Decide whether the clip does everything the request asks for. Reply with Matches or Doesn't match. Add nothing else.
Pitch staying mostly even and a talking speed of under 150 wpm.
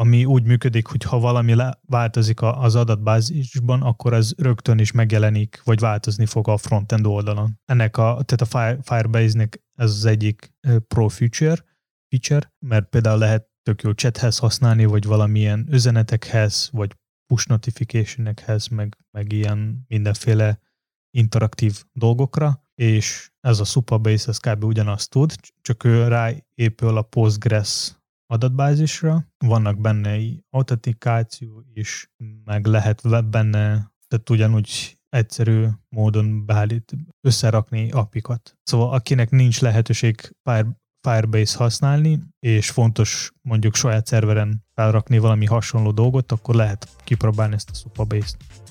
Matches